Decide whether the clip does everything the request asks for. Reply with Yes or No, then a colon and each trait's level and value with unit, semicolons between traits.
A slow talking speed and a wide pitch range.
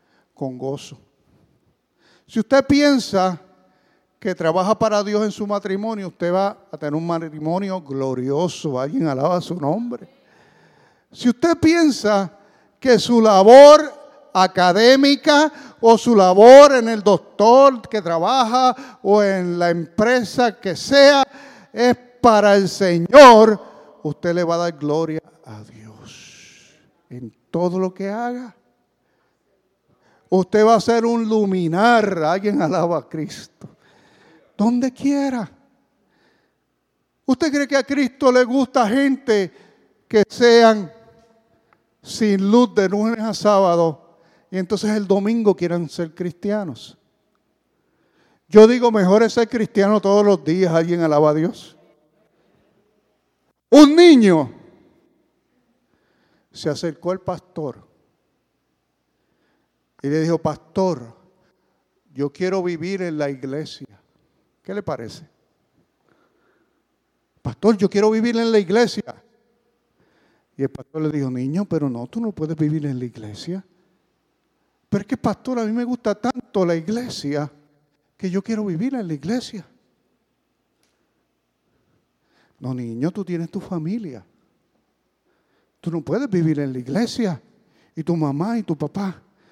Yes: slow, 125 wpm; wide, 6.0 semitones